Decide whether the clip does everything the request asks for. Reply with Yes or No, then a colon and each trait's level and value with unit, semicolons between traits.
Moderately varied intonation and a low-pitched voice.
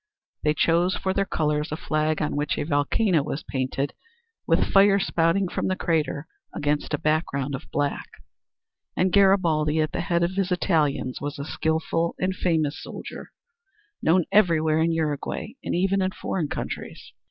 No: average, 3.6 semitones; medium, 160 Hz